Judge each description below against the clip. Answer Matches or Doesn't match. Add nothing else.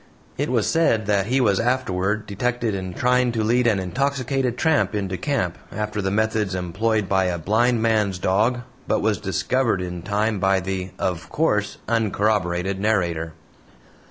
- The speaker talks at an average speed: Matches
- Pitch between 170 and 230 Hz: Doesn't match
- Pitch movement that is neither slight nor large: Matches